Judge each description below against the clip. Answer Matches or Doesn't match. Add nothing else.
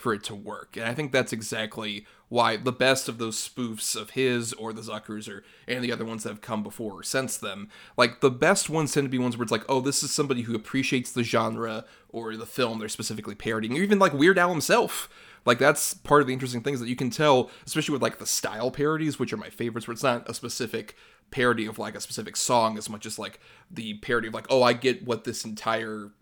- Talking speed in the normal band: Doesn't match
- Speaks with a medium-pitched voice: Doesn't match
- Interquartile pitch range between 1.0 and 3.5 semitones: Matches